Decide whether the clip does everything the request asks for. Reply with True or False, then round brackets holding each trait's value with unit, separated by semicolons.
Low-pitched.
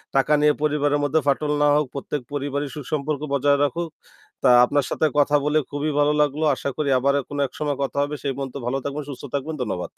False (145 Hz)